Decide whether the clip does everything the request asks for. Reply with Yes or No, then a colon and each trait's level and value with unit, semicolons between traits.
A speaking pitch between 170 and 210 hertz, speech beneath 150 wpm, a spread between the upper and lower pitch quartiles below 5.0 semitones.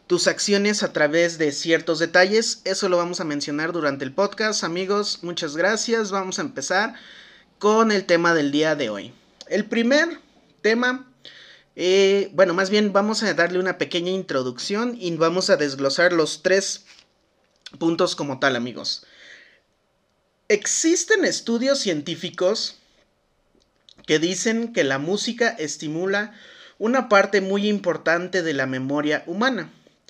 Yes: medium, 185 Hz; average, 135 wpm; average, 4.1 semitones